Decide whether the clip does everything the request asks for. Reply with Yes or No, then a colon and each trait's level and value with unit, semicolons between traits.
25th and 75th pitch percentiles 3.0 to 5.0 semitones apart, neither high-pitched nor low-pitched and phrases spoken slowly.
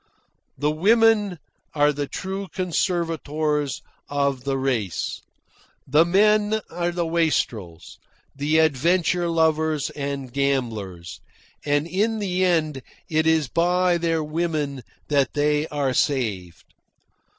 Yes: average, 3.7 semitones; medium, 155 Hz; slow, 110 wpm